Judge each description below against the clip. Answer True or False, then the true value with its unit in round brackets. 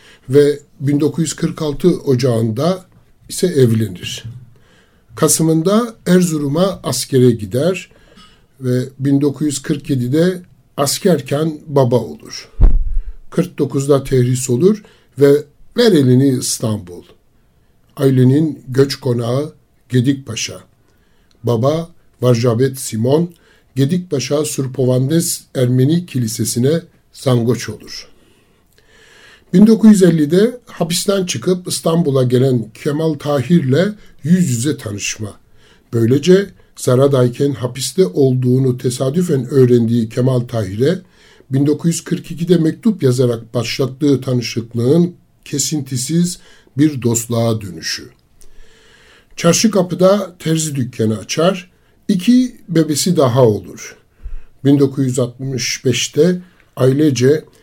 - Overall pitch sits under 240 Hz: True (140 Hz)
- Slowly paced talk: True (75 wpm)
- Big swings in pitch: False (4.8 semitones)